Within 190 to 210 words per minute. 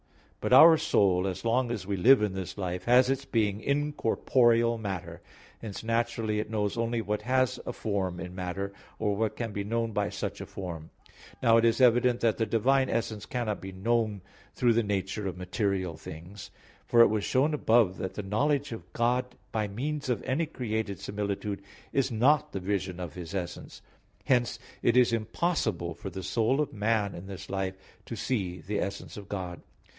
Yes: average, 195 wpm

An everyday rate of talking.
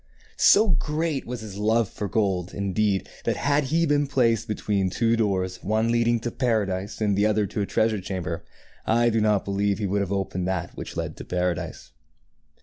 Yes: average, 190 wpm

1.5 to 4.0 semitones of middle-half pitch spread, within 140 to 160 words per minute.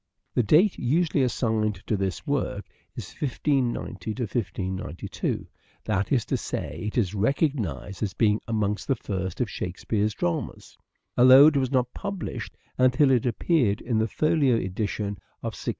No: average, 4.8 semitones; average, 150 wpm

